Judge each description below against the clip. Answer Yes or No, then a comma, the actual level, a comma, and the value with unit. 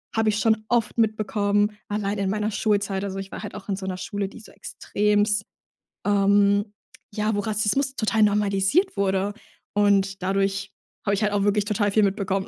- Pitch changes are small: Yes, narrow, 1.3 semitones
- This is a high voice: Yes, high, 205 Hz